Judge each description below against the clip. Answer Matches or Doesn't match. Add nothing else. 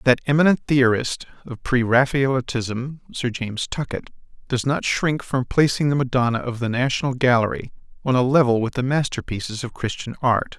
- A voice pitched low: Matches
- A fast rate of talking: Doesn't match